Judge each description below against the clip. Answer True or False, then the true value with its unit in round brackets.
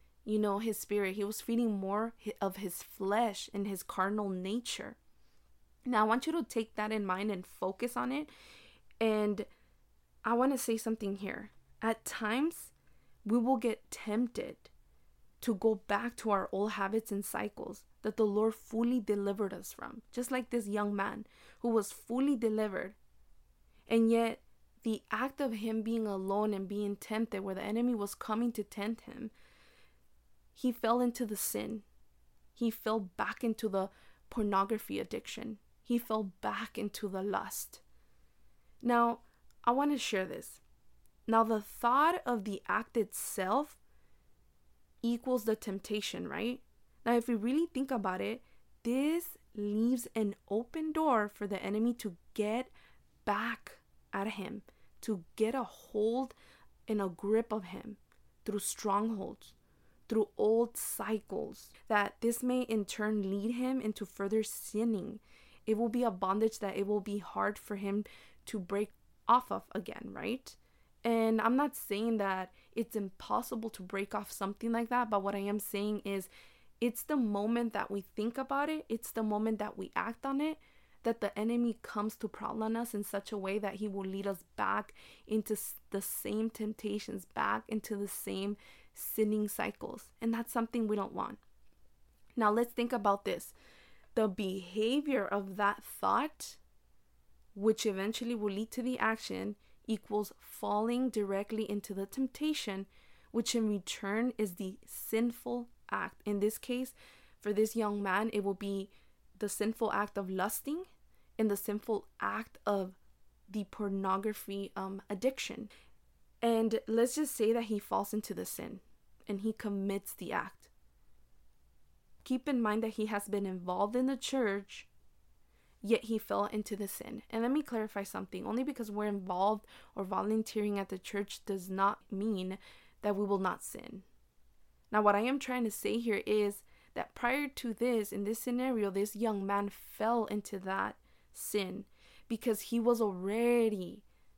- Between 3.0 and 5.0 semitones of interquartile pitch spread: False (2.5 semitones)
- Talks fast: False (160 wpm)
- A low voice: False (215 Hz)